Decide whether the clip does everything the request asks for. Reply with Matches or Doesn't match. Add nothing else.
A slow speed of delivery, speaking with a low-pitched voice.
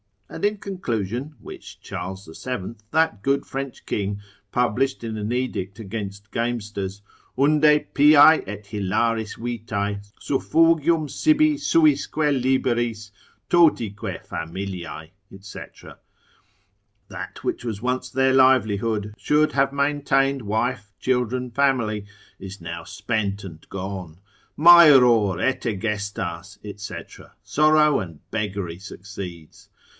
Matches